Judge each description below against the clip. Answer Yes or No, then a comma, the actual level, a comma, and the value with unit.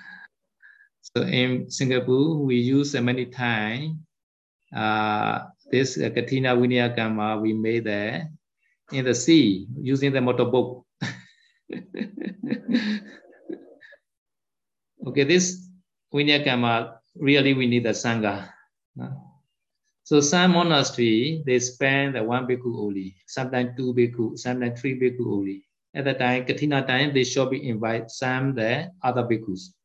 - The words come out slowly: Yes, slow, 120 wpm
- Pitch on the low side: Yes, low, 125 Hz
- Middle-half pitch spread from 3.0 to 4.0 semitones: Yes, average, 3.7 semitones